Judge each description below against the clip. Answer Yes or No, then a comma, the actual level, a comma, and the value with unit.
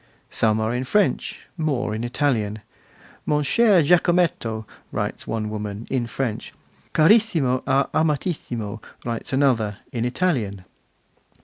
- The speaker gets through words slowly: Yes, slow, 115 wpm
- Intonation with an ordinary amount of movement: No, wide, 5.9 semitones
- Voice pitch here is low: Yes, low, 125 Hz